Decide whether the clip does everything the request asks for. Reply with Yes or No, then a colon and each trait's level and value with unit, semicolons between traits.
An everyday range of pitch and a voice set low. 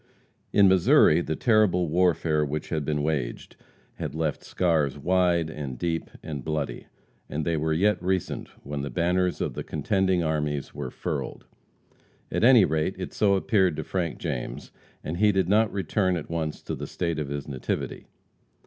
Yes: average, 3.6 semitones; very low, 80 Hz